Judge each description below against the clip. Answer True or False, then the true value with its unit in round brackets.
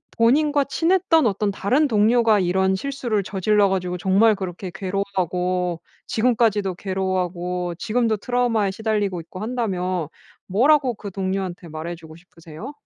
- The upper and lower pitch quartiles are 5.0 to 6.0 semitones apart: False (4.0 semitones)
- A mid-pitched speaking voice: False (195 Hz)